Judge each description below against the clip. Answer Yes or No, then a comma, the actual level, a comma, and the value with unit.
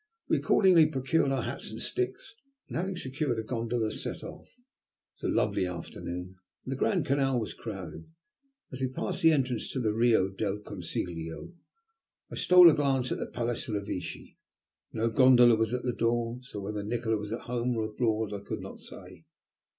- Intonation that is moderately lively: Yes, average, 3.9 semitones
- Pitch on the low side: Yes, low, 115 Hz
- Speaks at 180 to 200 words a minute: Yes, average, 185 wpm